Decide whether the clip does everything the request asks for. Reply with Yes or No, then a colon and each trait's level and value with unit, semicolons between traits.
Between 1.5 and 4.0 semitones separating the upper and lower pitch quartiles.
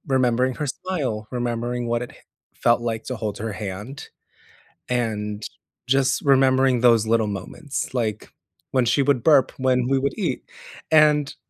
Yes: average, 2.8 semitones